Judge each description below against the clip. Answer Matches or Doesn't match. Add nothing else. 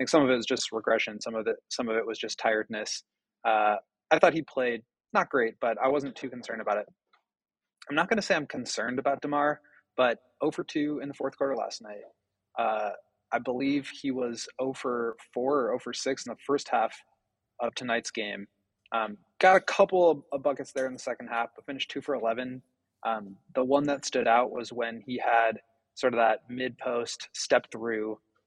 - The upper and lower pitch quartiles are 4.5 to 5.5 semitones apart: Doesn't match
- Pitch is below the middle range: Matches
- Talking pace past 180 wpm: Matches